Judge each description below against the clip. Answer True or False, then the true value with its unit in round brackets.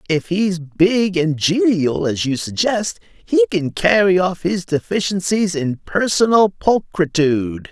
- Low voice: False (180 Hz)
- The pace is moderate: False (130 wpm)